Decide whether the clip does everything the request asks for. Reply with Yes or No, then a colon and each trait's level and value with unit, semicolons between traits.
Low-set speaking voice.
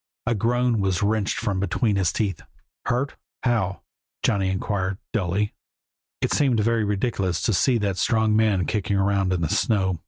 Yes: low, 100 Hz